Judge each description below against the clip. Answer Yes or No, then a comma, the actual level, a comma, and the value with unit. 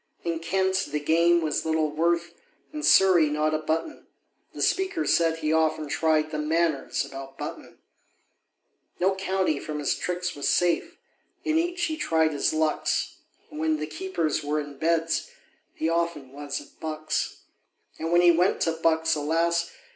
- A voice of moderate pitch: Yes, medium, 160 Hz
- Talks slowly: No, average, 160 wpm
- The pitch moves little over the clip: Yes, narrow, 2.1 semitones